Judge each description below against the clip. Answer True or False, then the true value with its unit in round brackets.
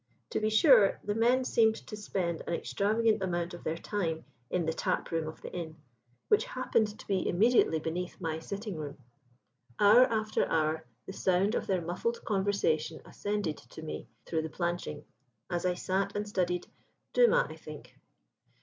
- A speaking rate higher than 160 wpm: True (170 wpm)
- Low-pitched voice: False (185 Hz)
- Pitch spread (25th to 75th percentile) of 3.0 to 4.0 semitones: False (4.7 semitones)